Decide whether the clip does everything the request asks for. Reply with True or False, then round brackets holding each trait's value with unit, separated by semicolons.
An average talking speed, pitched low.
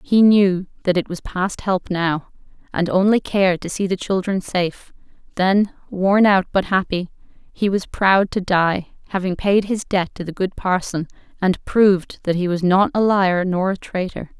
False (190 wpm; 185 Hz)